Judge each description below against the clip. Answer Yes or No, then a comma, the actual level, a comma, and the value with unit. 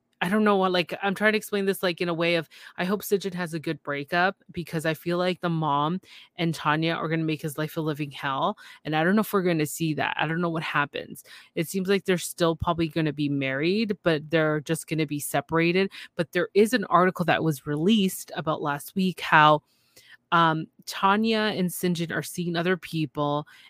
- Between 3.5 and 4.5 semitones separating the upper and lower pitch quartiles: No, average, 3.1 semitones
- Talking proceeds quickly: Yes, fast, 230 wpm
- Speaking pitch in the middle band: Yes, medium, 170 Hz